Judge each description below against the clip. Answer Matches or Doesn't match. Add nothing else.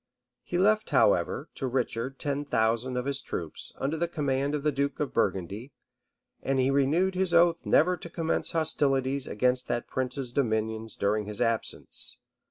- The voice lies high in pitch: Doesn't match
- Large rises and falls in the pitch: Doesn't match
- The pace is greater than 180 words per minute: Doesn't match